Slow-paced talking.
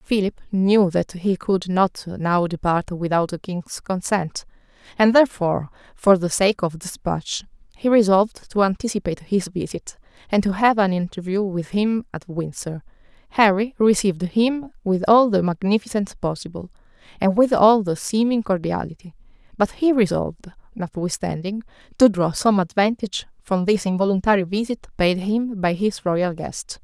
No: average, 150 wpm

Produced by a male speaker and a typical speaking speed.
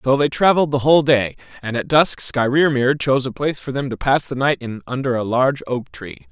No: male; fast, 235 wpm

